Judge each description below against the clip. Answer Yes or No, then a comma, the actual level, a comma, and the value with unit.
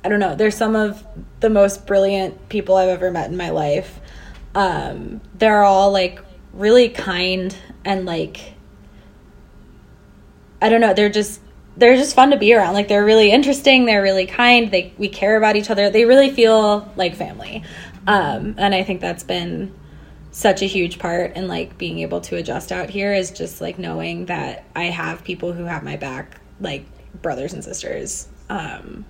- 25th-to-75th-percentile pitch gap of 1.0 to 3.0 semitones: No, average, 3.4 semitones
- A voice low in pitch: No, high, 195 Hz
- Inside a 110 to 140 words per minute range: No, average, 180 wpm